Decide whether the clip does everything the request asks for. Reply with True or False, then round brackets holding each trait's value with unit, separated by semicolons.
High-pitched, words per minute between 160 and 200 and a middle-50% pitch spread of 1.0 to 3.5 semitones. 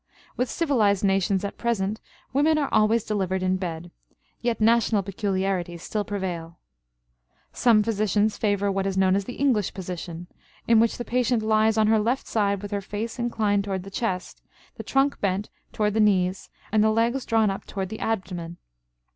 True (205 Hz; 175 wpm; 2.9 semitones)